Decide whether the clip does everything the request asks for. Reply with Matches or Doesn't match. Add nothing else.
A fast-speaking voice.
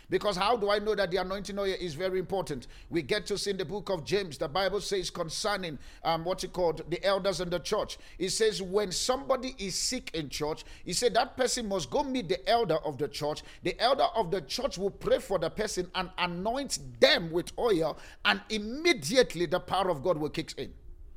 Matches